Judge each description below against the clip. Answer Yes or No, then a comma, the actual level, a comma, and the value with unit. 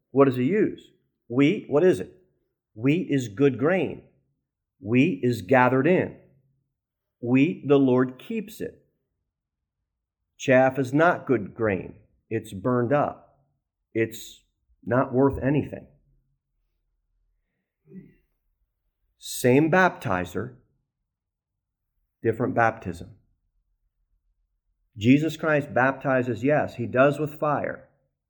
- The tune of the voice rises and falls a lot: Yes, wide, 6.1 semitones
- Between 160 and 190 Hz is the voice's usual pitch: No, low, 125 Hz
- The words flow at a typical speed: No, slow, 95 wpm